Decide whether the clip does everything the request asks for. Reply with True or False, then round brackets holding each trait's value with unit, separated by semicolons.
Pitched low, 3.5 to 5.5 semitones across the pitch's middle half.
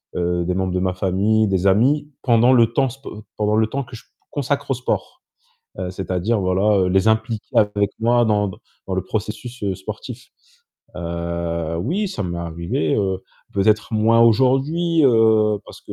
True (105 Hz; 4.4 semitones)